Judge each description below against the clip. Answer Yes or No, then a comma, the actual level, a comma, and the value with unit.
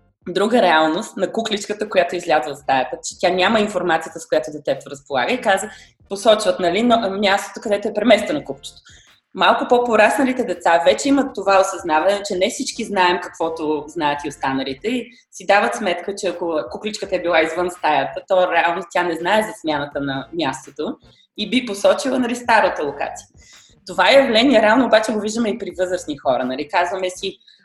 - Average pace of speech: No, fast, 175 wpm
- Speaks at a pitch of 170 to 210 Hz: Yes, high, 190 Hz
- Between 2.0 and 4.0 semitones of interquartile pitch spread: No, average, 4.6 semitones